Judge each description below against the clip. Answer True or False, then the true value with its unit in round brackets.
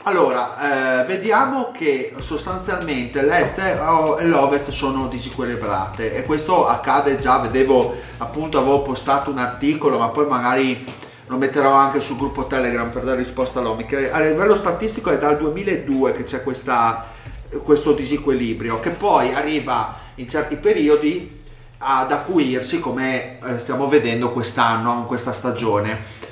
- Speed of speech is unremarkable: True (135 wpm)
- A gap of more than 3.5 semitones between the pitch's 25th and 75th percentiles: False (3.2 semitones)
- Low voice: True (130 Hz)